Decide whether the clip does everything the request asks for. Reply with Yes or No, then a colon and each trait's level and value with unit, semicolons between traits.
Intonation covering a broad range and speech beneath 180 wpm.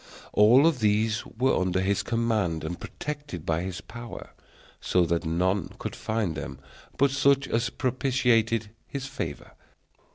Yes: wide, 5.8 semitones; slow, 135 wpm